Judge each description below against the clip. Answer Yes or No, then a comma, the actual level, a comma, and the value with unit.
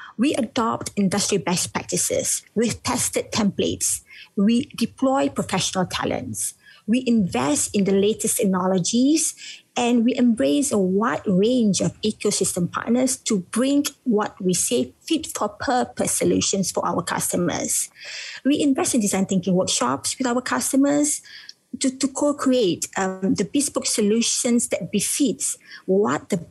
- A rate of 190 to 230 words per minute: No, slow, 135 wpm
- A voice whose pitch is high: Yes, high, 230 Hz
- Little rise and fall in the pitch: No, wide, 5.4 semitones